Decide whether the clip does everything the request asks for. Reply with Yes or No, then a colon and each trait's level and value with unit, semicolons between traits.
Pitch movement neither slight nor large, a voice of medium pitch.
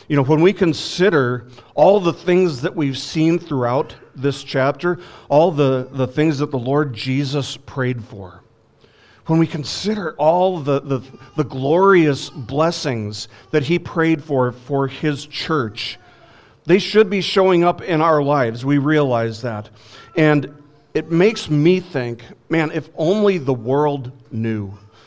Yes: average, 4.3 semitones; medium, 145 Hz